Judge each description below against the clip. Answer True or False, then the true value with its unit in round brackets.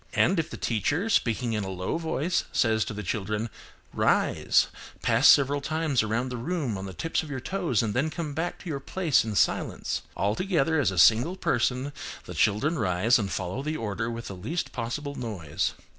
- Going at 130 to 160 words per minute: False (200 wpm)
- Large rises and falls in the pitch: True (6.4 semitones)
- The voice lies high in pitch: False (125 Hz)